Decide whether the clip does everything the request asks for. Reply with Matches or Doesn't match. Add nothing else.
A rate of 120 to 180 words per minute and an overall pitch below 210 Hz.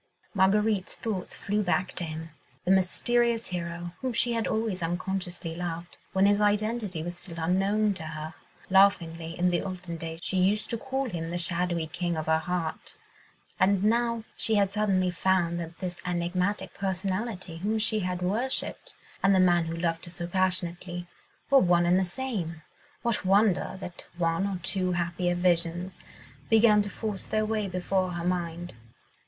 Matches